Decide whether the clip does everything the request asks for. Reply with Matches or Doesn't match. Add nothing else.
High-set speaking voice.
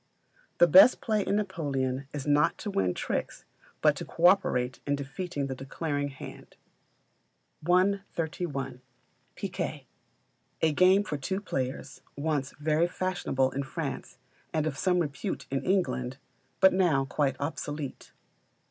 Doesn't match